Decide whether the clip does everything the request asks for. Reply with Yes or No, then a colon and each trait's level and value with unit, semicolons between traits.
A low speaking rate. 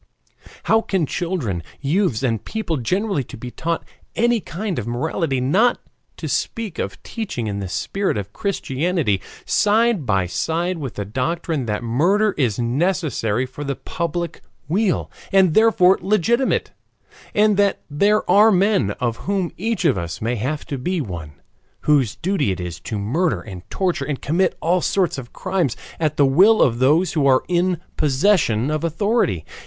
No: average, 160 wpm